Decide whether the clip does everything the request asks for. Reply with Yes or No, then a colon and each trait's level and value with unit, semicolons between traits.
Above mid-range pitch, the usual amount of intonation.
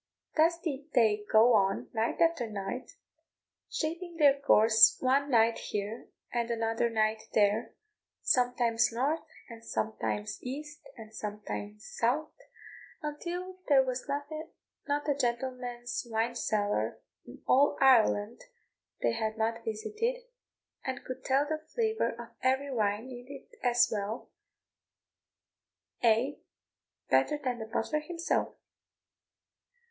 Yes: high, 245 Hz; average, 4.5 semitones